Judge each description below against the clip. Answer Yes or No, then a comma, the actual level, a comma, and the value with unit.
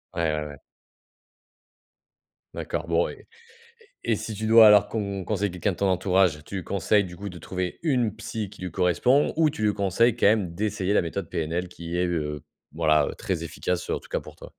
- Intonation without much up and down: No, average, 3.7 semitones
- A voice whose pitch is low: Yes, very low, 95 Hz